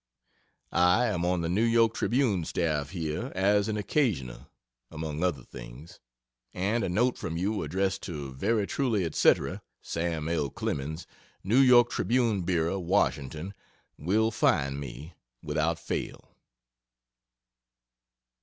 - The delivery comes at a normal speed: No, slow, 125 wpm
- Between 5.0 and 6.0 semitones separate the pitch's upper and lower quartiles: Yes, wide, 5.5 semitones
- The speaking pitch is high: No, very low, 90 Hz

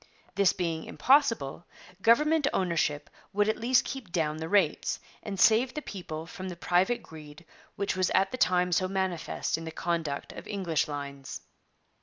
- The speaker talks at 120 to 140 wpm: No, average, 165 wpm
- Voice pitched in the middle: Yes, medium, 180 Hz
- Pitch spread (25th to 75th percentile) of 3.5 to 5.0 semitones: Yes, average, 4.3 semitones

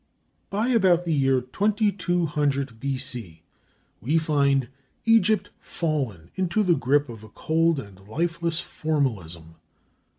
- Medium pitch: Yes, medium, 145 Hz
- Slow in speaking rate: Yes, slow, 110 wpm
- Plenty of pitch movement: Yes, wide, 5.7 semitones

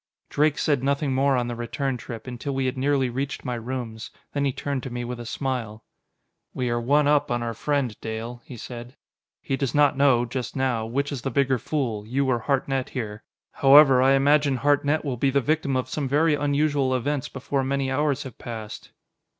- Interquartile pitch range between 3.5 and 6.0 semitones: No, average, 2.7 semitones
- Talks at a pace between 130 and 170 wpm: No, fast, 205 wpm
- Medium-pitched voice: No, low, 130 Hz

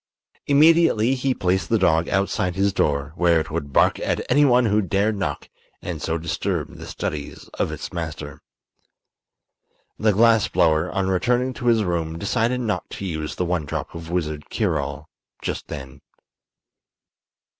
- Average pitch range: No, wide, 6.1 semitones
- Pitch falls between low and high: No, very low, 90 Hz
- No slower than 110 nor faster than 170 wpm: Yes, average, 155 wpm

